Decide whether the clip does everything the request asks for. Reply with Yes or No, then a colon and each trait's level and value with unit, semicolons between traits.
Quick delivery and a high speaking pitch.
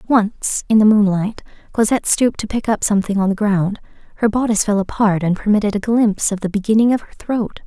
Yes: fast, 210 wpm; high, 210 Hz